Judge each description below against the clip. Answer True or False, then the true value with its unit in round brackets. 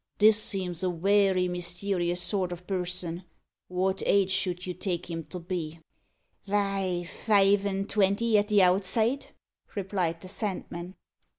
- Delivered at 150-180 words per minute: False (135 wpm)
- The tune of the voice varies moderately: False (2.1 semitones)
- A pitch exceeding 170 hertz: True (185 Hz)